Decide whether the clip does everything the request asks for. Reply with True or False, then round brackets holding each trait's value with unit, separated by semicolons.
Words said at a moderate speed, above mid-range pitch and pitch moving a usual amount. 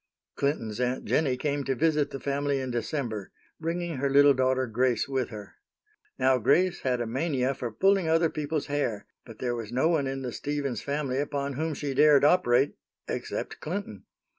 False (180 wpm; 140 Hz; 3.0 semitones)